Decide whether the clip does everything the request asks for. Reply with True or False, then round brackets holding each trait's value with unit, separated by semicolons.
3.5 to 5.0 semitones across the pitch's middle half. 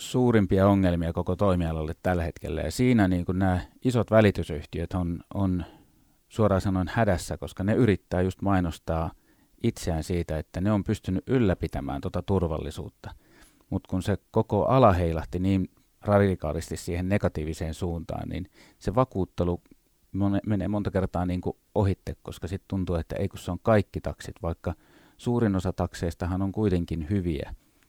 False (2.9 semitones)